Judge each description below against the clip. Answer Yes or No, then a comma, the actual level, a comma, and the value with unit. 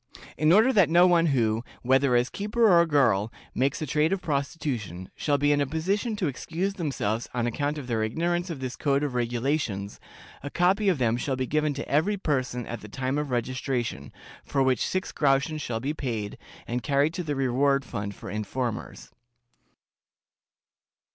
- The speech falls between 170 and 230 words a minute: Yes, average, 180 wpm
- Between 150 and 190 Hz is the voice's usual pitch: No, medium, 140 Hz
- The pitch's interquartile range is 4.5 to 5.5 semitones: Yes, average, 4.8 semitones